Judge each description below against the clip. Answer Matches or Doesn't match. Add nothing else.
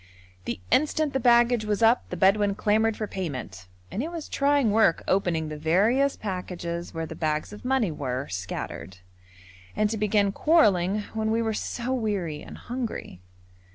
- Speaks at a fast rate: Doesn't match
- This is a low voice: Doesn't match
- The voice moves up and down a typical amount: Doesn't match